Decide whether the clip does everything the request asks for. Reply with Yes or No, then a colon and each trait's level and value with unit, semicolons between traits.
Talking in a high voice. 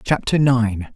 No: low, 120 Hz